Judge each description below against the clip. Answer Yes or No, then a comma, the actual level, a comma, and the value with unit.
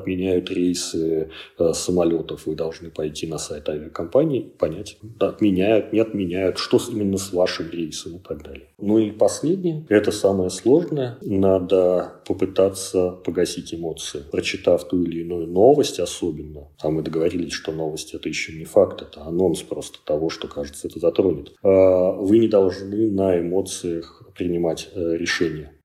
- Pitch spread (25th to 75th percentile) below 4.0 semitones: Yes, average, 2.8 semitones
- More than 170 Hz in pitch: No, very low, 90 Hz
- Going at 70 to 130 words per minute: No, average, 150 wpm